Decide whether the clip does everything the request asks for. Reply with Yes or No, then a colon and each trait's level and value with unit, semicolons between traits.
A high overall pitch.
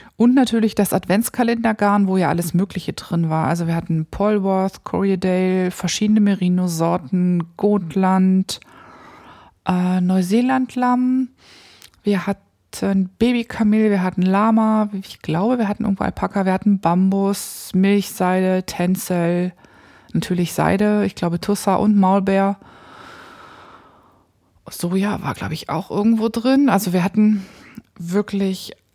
Yes: high, 195 Hz